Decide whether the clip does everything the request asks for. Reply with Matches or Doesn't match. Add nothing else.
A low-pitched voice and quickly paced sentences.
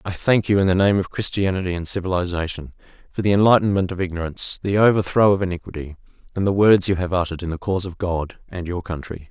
Matches